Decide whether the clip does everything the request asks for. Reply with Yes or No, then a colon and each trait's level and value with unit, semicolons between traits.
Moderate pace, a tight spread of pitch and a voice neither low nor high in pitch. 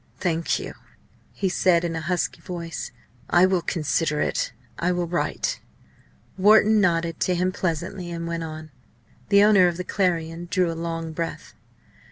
Yes: average, 155 wpm; narrow, 1.8 semitones; medium, 170 Hz